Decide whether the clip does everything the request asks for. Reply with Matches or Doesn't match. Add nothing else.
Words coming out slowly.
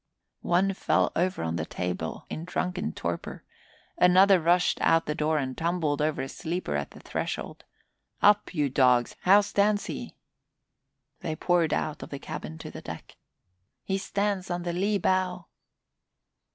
Doesn't match